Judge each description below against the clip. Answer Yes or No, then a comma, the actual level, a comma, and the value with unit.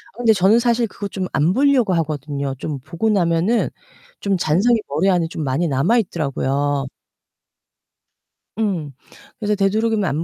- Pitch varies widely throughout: Yes, wide, 6.6 semitones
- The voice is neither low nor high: Yes, medium, 180 Hz